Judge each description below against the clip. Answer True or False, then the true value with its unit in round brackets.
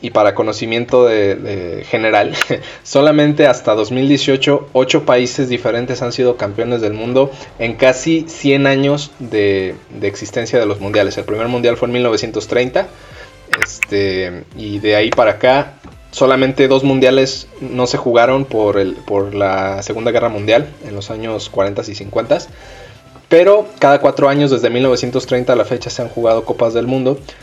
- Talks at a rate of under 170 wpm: True (160 wpm)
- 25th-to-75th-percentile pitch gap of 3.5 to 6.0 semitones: True (4.1 semitones)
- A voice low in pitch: True (125 Hz)